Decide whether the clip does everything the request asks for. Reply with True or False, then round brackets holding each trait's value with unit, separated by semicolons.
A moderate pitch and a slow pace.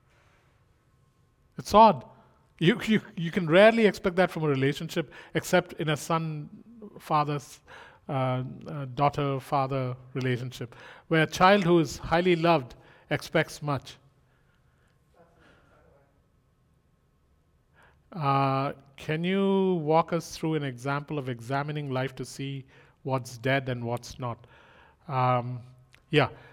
True (145 Hz; 115 wpm)